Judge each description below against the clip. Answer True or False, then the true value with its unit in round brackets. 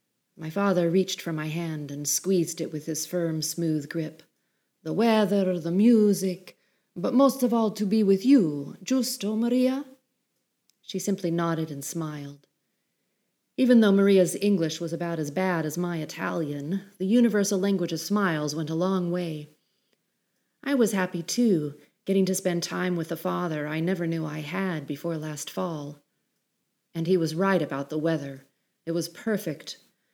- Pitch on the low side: False (180 Hz)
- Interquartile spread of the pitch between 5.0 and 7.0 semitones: False (3.9 semitones)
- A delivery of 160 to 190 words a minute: True (165 wpm)